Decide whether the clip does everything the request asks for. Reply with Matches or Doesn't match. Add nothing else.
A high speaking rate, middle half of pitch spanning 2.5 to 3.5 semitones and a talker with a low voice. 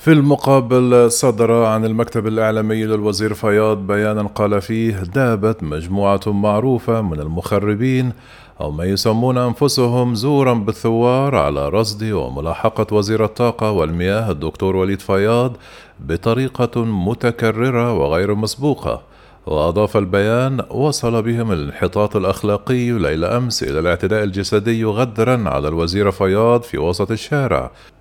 Doesn't match